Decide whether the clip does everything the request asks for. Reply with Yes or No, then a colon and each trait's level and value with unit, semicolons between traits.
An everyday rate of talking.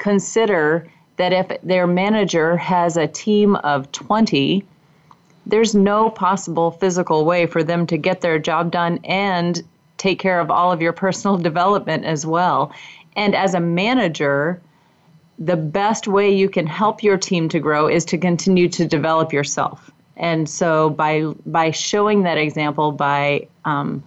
Yes: average, 155 wpm